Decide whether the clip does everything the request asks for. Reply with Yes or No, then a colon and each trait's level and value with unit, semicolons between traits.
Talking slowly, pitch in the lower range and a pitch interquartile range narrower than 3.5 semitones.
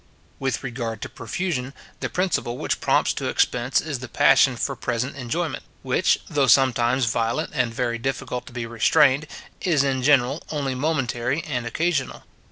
No: average, 160 wpm; low, 130 Hz; average, 3.1 semitones